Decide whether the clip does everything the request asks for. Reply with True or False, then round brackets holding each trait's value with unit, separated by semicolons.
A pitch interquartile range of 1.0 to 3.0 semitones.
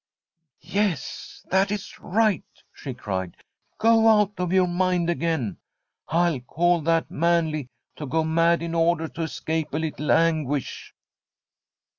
True (2.5 semitones)